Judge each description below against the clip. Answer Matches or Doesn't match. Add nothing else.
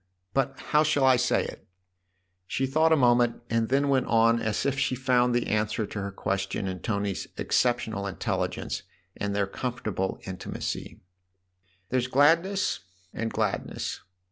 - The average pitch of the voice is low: Matches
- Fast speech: Doesn't match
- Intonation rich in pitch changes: Doesn't match